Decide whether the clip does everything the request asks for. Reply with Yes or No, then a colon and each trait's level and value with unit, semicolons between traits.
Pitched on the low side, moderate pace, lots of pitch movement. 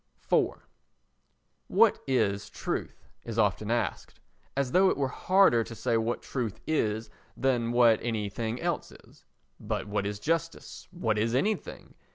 No: low, 115 Hz; average, 145 wpm; average, 3.7 semitones